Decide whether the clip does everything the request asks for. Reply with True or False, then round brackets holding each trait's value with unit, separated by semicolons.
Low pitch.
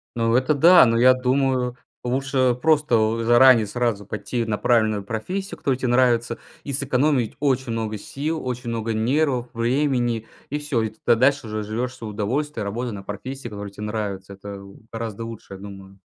True (120 Hz)